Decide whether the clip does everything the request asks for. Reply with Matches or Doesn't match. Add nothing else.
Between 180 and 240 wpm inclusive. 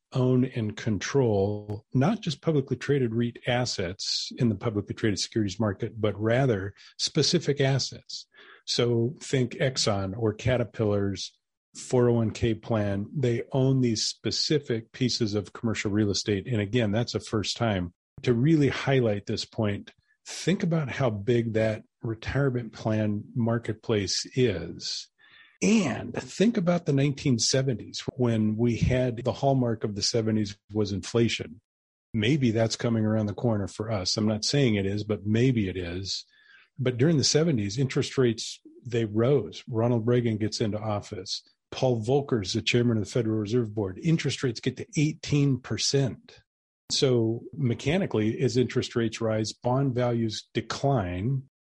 Doesn't match